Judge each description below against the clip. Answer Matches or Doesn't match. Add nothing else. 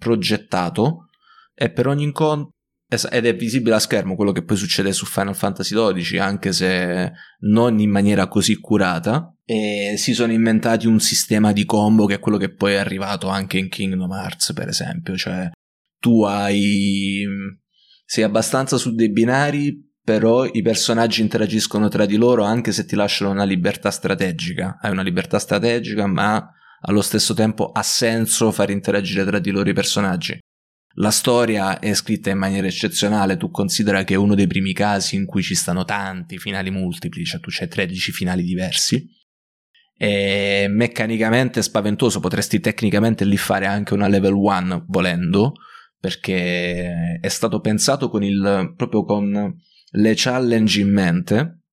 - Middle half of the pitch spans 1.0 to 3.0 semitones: Matches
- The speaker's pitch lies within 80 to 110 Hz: Matches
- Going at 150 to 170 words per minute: Matches